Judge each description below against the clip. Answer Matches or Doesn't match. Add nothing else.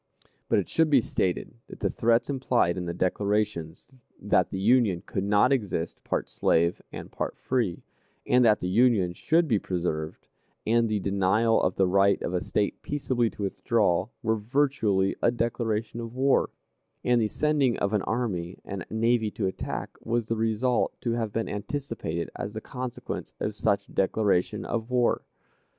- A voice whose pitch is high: Doesn't match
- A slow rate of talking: Doesn't match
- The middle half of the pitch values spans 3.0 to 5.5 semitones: Matches